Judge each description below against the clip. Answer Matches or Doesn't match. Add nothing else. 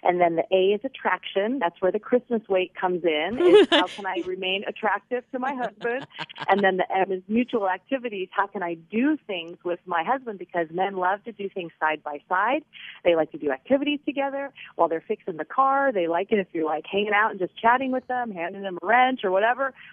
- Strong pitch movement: Matches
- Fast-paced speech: Matches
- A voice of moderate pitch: Doesn't match